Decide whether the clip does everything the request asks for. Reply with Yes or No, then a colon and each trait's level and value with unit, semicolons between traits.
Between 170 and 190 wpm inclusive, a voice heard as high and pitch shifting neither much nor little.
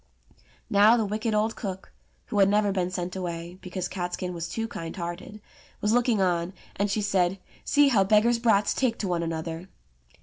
Yes: average, 180 wpm; high, 195 Hz; average, 3.3 semitones